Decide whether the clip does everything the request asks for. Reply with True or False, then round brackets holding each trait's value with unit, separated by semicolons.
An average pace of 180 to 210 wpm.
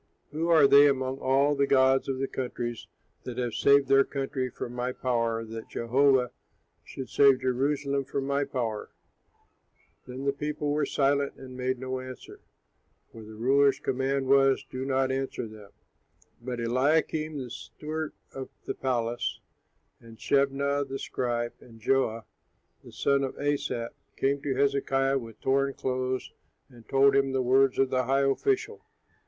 False (155 wpm)